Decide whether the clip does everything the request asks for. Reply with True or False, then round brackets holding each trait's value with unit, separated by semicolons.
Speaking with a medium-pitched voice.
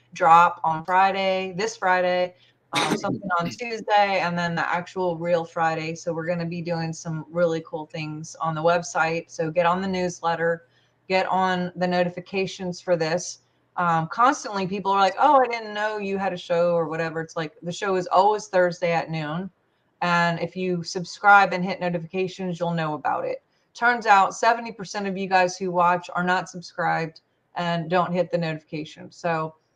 True (175 Hz)